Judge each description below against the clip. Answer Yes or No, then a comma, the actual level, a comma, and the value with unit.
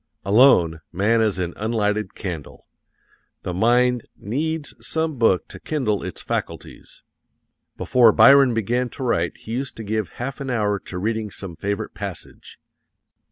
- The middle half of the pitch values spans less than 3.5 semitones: No, average, 4.1 semitones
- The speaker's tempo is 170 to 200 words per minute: No, average, 145 wpm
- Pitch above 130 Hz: No, low, 110 Hz